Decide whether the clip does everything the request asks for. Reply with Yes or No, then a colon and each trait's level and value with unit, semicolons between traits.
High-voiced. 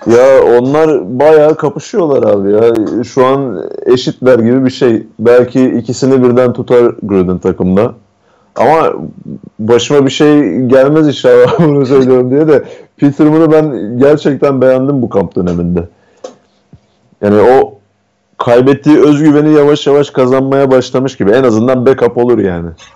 No: low, 130 Hz